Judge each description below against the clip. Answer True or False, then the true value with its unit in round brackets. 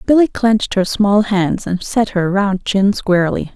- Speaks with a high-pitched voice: True (200 Hz)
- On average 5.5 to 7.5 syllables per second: False (4.4 syllables/s)